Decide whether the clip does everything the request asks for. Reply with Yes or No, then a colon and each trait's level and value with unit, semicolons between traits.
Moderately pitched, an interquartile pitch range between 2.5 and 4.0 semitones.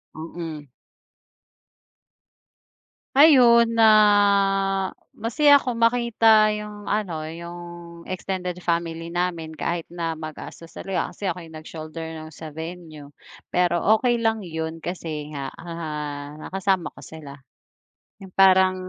No: medium, 175 Hz; average, 4.5 semitones